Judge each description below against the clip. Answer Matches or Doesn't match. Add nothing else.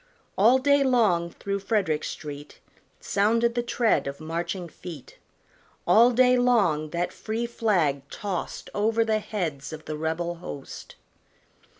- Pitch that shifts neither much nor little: Doesn't match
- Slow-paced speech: Matches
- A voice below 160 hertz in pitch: Doesn't match